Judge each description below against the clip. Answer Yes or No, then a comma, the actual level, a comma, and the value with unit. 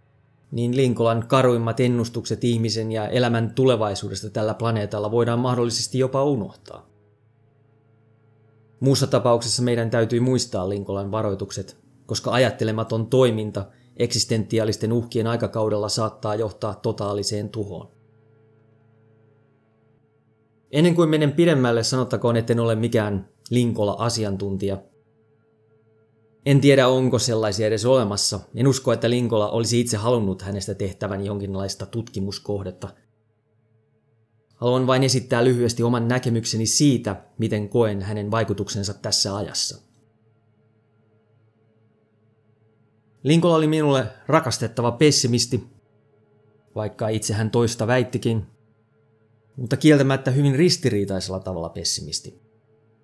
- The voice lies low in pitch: Yes, low, 110 Hz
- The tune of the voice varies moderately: No, narrow, 2.2 semitones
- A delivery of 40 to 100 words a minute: Yes, slow, 95 wpm